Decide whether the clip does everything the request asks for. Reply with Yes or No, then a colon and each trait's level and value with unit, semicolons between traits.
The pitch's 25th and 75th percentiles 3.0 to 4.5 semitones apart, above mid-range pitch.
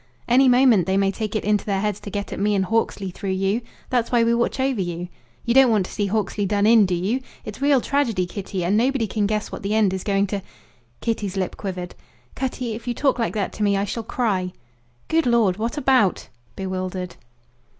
Yes: average, 3.5 semitones; high, 210 Hz